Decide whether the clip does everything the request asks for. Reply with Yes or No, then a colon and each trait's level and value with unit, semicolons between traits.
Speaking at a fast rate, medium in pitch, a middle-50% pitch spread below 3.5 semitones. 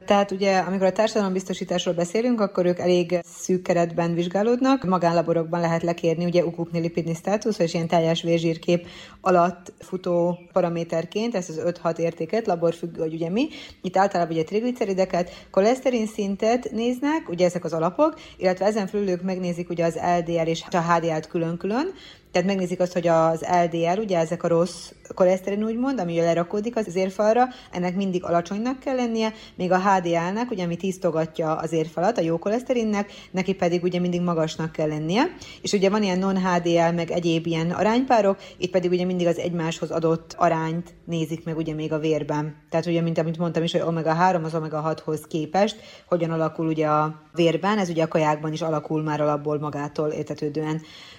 Yes: fast, 170 wpm; medium, 175 Hz; average, 2.7 semitones